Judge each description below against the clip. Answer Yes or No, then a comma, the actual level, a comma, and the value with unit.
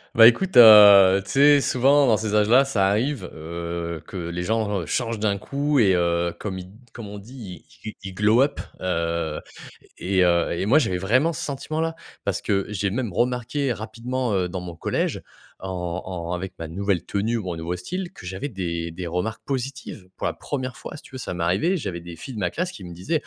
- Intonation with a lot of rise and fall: Yes, wide, 6.0 semitones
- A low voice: Yes, low, 100 Hz